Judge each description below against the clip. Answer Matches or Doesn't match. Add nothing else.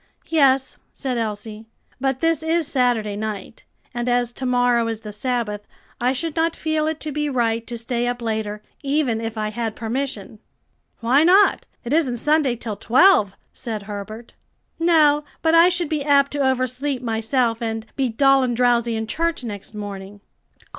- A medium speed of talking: Matches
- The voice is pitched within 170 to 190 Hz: Doesn't match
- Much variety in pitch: Doesn't match